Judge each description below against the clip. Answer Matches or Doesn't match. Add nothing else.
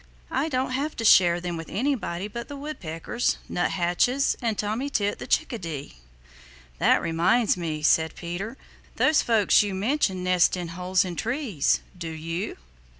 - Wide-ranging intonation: Matches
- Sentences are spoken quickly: Doesn't match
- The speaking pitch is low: Doesn't match